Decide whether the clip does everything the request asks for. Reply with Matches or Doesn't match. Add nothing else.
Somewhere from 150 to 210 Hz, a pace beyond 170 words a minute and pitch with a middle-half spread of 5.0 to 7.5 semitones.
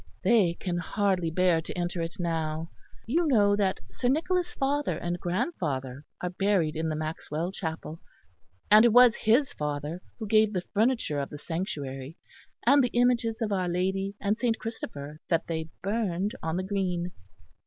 Doesn't match